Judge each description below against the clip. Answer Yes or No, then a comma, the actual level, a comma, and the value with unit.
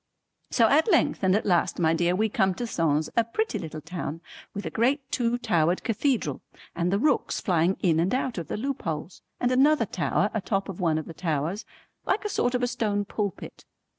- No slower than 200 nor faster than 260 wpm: Yes, fast, 205 wpm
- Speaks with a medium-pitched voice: No, high, 200 Hz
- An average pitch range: No, wide, 6.2 semitones